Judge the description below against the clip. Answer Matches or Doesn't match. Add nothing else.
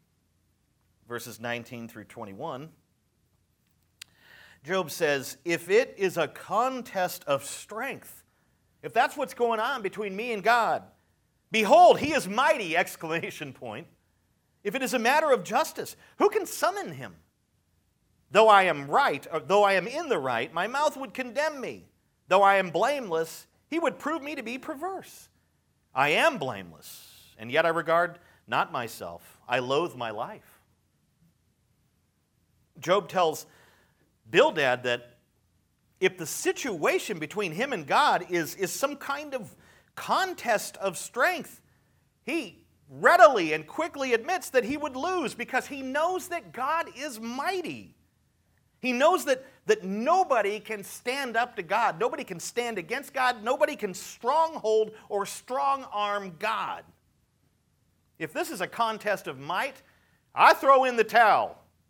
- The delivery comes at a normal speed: Matches